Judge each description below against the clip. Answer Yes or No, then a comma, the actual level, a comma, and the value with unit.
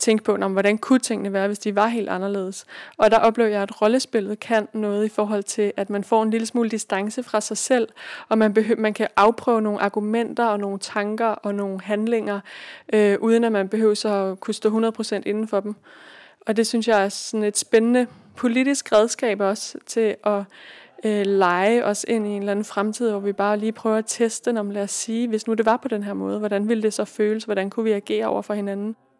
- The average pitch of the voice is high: Yes, high, 215 Hz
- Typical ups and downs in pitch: No, narrow, 1.9 semitones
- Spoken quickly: Yes, fast, 230 wpm